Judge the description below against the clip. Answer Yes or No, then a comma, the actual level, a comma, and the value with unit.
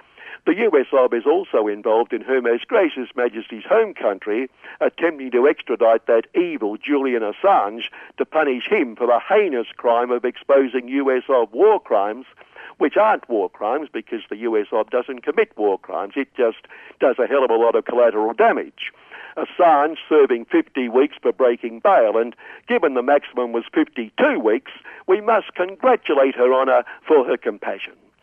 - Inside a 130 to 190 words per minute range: Yes, average, 165 wpm